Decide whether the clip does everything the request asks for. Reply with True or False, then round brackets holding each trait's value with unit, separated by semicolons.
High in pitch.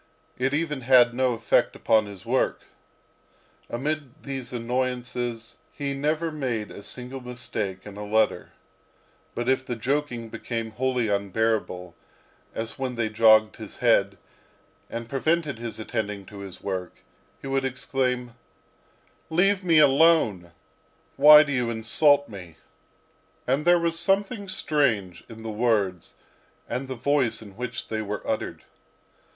False (120 Hz)